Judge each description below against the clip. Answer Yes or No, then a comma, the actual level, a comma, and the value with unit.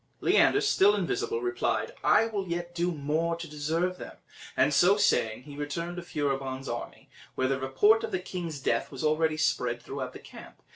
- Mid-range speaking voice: Yes, medium, 170 Hz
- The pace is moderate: Yes, average, 185 wpm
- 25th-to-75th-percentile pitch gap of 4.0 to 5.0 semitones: Yes, average, 4.5 semitones